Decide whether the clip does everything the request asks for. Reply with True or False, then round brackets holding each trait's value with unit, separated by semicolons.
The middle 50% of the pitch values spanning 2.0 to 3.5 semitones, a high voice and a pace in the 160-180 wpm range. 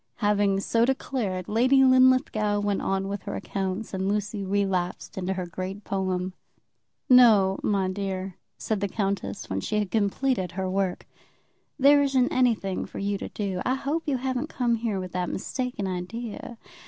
False (4.3 semitones; 205 Hz; 165 wpm)